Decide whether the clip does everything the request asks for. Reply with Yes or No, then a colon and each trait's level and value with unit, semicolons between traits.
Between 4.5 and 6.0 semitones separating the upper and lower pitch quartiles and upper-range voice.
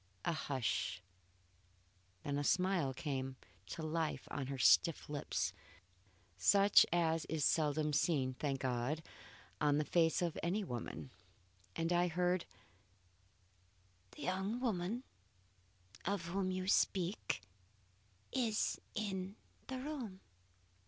No: average, 4.8 semitones; medium, 165 Hz